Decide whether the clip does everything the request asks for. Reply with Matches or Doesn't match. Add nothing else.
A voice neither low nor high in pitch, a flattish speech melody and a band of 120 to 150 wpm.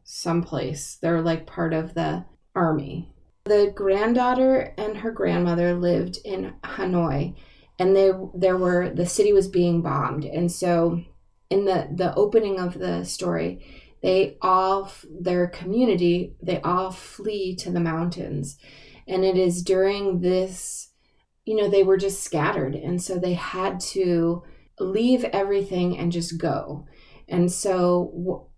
Matches